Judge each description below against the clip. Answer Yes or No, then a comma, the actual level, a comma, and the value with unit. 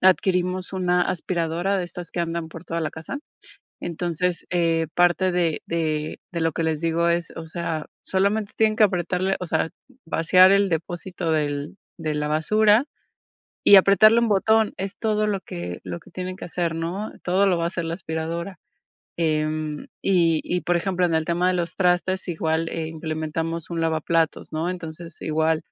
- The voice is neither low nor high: Yes, medium, 170 Hz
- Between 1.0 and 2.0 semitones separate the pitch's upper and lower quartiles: No, narrow, 2.4 semitones